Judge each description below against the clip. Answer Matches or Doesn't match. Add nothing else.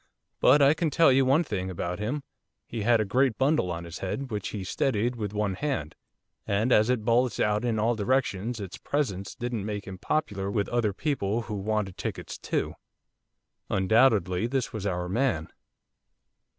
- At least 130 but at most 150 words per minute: Doesn't match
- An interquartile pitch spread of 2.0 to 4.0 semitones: Doesn't match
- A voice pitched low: Matches